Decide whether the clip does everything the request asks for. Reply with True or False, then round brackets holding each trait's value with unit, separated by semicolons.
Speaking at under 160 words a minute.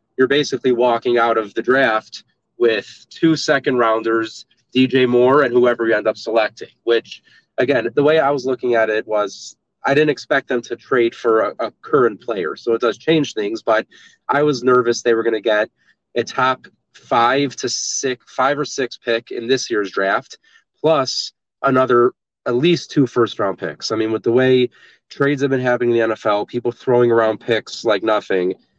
False (195 wpm)